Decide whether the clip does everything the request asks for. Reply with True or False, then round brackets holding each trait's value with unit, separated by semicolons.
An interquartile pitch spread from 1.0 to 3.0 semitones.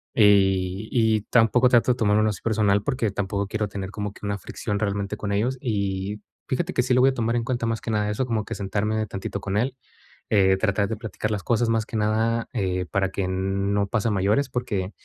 True (2.4 semitones)